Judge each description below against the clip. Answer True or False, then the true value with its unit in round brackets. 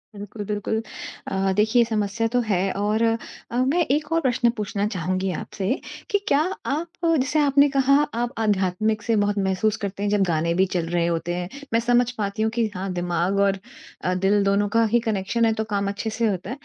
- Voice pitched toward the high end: True (205 Hz)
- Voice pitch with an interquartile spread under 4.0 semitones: True (3.3 semitones)